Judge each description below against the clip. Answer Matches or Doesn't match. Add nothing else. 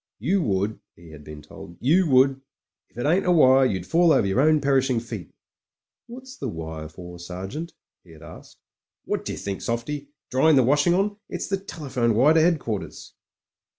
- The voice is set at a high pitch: Doesn't match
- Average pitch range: Doesn't match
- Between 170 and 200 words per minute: Matches